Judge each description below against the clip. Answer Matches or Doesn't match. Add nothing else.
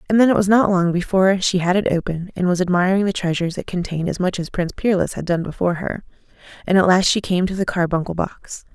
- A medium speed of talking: Doesn't match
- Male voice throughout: Doesn't match